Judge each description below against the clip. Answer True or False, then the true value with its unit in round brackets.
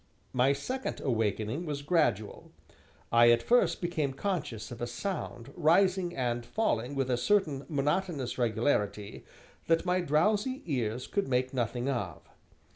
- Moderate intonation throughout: False (6.6 semitones)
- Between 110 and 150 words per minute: True (135 wpm)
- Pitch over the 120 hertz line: True (135 Hz)